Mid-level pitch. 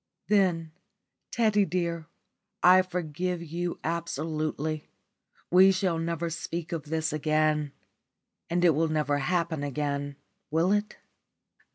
Yes: medium, 165 Hz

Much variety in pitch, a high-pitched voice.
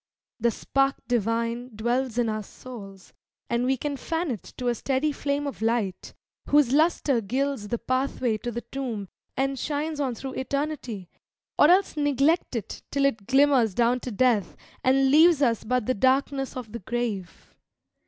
No: average, 3.3 semitones; very high, 255 Hz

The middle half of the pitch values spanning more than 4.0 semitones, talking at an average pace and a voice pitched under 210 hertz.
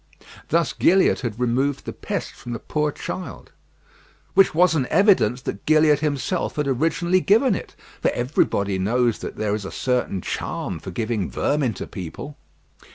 Yes: wide, 5.6 semitones; average, 160 wpm; low, 135 Hz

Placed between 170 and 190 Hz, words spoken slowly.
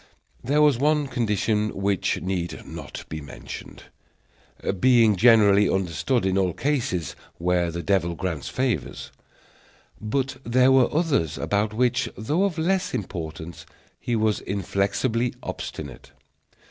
No: low, 105 Hz; slow, 120 wpm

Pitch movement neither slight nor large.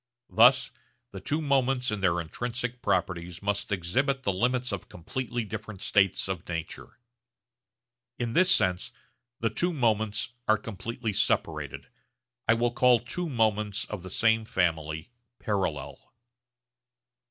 Yes: average, 4.7 semitones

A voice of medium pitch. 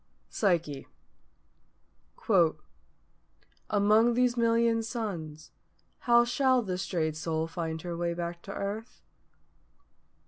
No: high, 195 Hz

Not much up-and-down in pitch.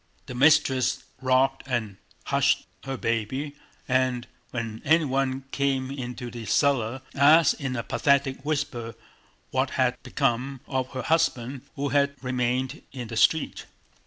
Yes: narrow, 2.2 semitones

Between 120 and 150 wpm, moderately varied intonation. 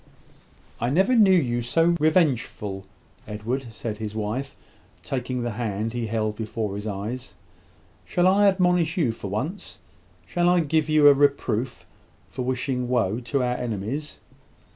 No: average, 145 wpm; wide, 5.9 semitones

